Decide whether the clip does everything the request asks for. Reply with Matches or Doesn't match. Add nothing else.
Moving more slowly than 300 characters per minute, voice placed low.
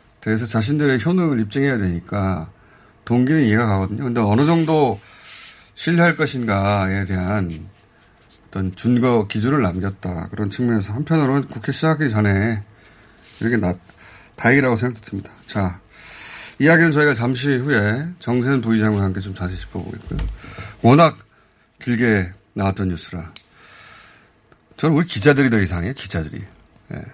Doesn't match